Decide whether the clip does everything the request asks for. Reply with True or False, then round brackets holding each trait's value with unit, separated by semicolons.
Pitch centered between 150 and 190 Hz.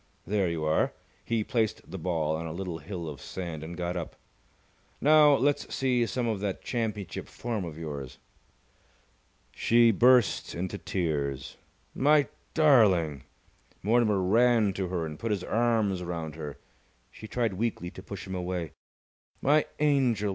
False (95 Hz)